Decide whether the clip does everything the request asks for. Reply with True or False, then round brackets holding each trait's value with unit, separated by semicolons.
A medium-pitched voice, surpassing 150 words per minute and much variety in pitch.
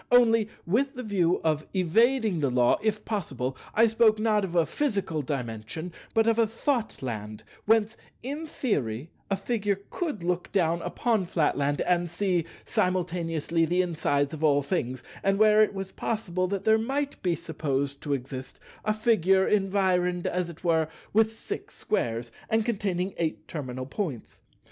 True (180 Hz; 160 wpm; 5.7 semitones)